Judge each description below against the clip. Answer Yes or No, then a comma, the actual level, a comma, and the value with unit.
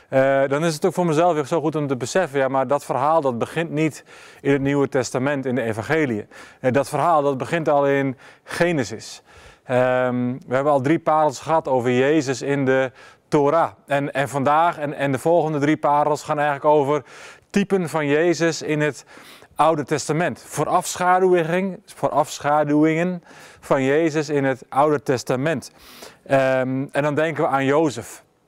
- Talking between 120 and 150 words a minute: No, average, 170 wpm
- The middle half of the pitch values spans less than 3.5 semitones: Yes, average, 2.8 semitones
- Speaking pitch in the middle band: Yes, medium, 145 Hz